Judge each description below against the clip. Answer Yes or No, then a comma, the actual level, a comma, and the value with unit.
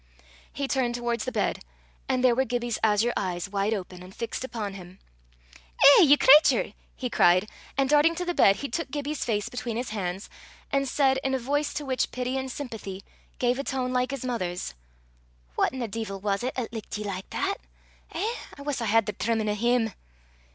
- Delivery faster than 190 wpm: Yes, average, 200 wpm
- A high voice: Yes, high, 240 Hz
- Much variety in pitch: No, average, 4.3 semitones